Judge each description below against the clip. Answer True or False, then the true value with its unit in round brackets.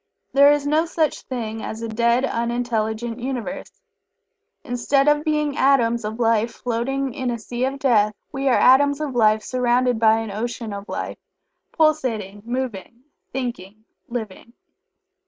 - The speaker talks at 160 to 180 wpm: False (145 wpm)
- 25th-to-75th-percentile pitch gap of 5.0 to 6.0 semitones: False (3.4 semitones)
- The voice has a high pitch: True (240 Hz)